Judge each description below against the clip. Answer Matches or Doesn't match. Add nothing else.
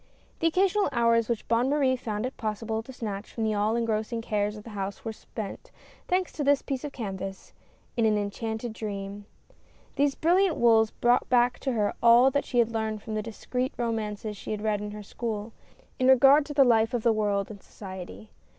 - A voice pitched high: Matches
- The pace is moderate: Doesn't match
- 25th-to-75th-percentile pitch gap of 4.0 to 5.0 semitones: Doesn't match